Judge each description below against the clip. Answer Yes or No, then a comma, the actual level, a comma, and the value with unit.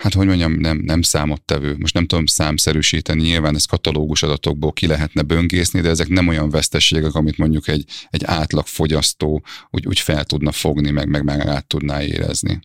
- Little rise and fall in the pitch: Yes, narrow, 1.9 semitones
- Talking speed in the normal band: No, fast, 180 wpm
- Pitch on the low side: Yes, very low, 80 Hz